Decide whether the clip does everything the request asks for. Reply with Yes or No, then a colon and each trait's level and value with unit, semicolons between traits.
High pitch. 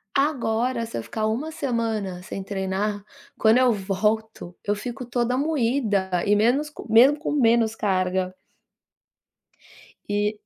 Yes: high, 220 Hz